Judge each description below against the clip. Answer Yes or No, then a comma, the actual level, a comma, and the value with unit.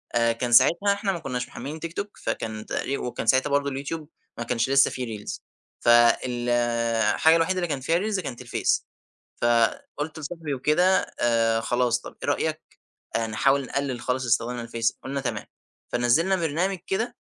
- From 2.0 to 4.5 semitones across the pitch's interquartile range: No, average, 5.3 semitones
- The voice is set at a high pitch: No, low, 130 Hz